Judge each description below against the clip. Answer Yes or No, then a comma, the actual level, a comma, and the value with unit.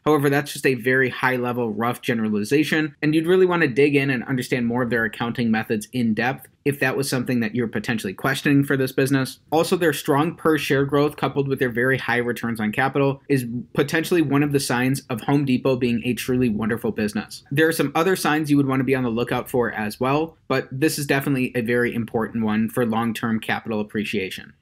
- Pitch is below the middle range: Yes, low, 130 Hz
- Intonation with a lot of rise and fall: No, average, 3.3 semitones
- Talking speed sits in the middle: No, fast, 220 wpm